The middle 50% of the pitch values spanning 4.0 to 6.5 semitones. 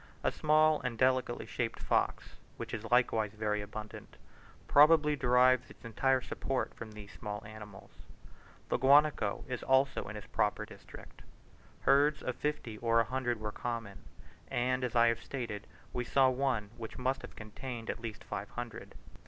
No: average, 3.4 semitones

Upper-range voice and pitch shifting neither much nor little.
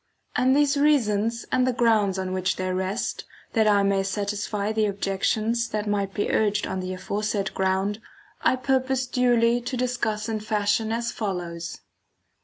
Yes: high, 210 Hz; average, 3.3 semitones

